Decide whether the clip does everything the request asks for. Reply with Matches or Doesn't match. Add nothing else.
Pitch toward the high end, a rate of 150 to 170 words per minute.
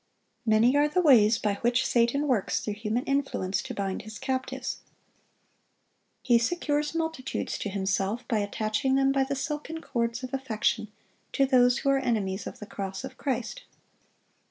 Matches